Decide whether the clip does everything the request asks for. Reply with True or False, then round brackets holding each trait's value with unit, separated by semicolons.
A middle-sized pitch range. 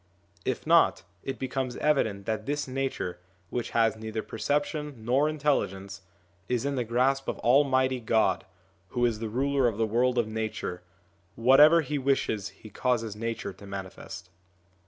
True (3.8 semitones)